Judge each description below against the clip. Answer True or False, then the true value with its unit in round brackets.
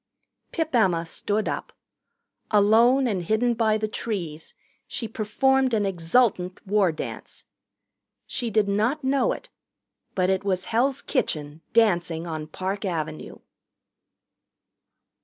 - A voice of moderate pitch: False (210 Hz)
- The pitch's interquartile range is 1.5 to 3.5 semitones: False (4.8 semitones)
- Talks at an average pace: False (120 wpm)